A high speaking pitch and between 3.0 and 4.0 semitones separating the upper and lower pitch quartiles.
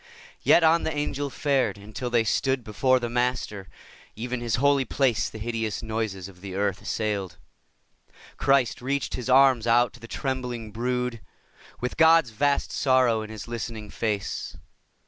No: low, 120 Hz; average, 3.3 semitones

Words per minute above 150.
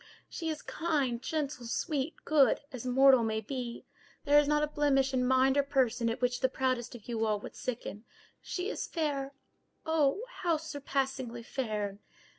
Yes: average, 165 wpm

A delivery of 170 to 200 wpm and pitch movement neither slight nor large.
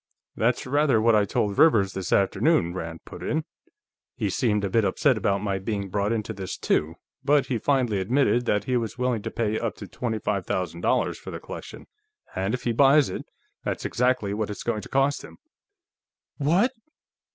Yes: average, 195 wpm; average, 4.3 semitones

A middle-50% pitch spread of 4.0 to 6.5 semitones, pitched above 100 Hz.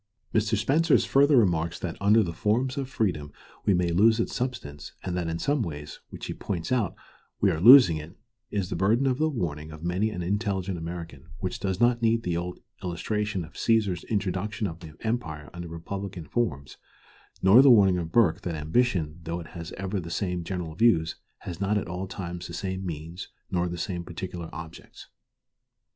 No: average, 4.3 semitones; very low, 90 Hz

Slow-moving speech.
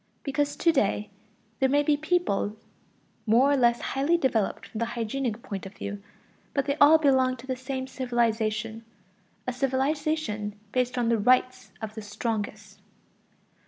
No: average, 155 wpm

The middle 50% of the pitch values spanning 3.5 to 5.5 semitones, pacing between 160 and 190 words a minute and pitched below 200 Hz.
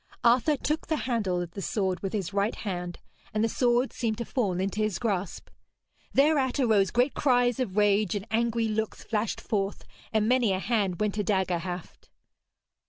No: average, 3.8 semitones; average, 180 wpm; high, 215 Hz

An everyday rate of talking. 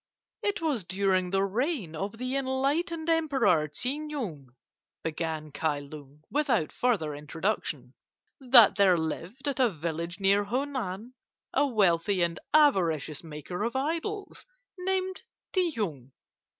No: slow, 125 wpm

